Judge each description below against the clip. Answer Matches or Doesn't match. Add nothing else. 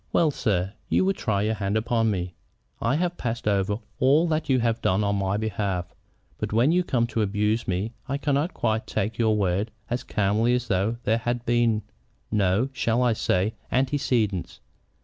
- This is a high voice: Doesn't match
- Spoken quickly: Doesn't match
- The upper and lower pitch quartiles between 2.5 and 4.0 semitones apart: Matches